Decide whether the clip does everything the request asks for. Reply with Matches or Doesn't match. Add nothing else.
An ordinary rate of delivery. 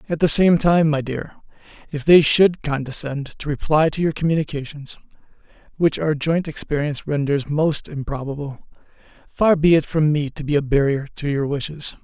Matches